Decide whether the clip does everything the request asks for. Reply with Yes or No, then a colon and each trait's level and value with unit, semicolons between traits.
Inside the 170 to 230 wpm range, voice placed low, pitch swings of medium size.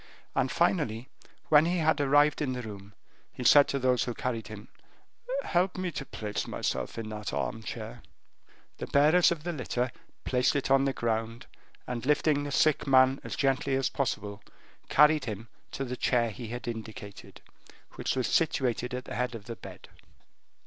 Yes: average, 175 wpm; low, 125 Hz; average, 3.9 semitones